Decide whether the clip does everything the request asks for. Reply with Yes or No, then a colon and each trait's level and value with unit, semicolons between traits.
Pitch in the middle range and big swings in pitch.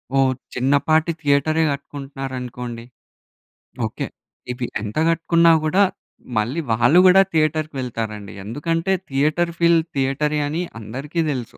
No: medium, 145 Hz; average, 4.6 semitones